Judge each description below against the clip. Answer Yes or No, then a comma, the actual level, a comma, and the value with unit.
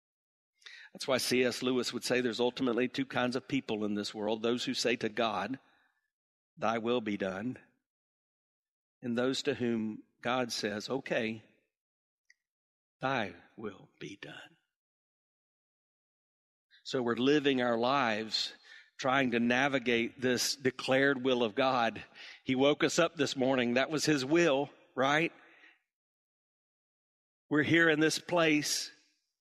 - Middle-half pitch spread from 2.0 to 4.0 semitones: Yes, average, 3.0 semitones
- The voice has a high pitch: No, low, 125 Hz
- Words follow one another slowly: Yes, slow, 130 wpm